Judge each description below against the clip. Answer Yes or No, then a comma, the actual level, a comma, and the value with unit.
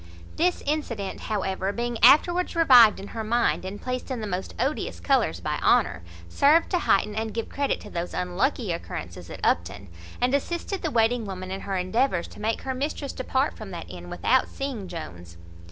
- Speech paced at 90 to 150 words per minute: No, average, 185 wpm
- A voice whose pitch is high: Yes, high, 230 Hz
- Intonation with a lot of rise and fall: Yes, wide, 6.2 semitones